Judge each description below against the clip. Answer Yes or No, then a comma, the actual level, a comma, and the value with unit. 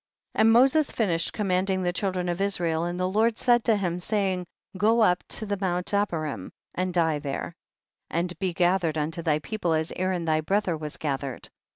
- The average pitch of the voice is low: No, medium, 180 Hz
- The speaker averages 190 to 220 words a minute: Yes, average, 195 wpm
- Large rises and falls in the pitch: No, average, 3.5 semitones